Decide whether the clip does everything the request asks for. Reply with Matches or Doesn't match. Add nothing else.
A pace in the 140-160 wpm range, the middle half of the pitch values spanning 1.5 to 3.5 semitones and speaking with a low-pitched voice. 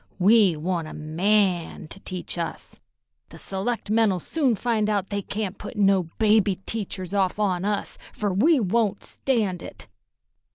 Doesn't match